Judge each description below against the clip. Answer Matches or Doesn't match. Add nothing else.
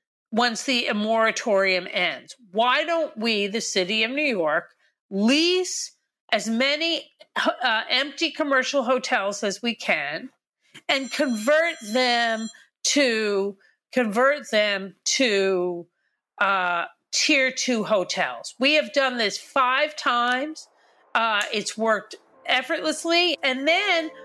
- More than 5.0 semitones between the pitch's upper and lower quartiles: Matches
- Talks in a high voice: Matches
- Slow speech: Matches